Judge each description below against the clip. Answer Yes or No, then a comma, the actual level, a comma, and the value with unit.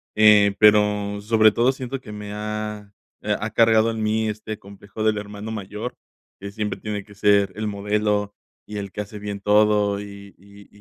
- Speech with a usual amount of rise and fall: No, narrow, 0.9 semitones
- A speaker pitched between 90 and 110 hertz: Yes, low, 105 Hz